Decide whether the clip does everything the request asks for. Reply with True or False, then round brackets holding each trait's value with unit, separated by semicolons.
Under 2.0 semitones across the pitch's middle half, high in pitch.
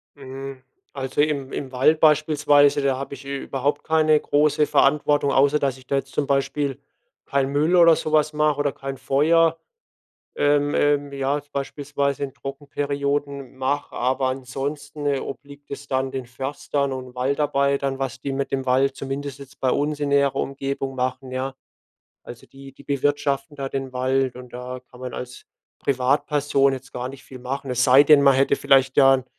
False (1.4 semitones; 140 Hz)